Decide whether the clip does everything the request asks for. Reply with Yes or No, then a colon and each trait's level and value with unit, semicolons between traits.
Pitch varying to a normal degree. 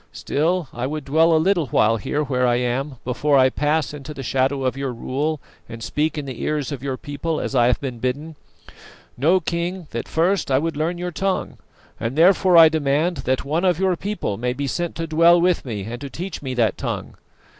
Yes: average, 4.3 semitones